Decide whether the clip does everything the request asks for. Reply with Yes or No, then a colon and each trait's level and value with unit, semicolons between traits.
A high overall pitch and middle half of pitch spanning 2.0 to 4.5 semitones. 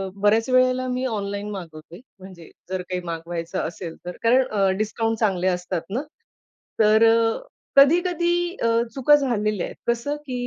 No: high, 215 Hz; wide, 5.5 semitones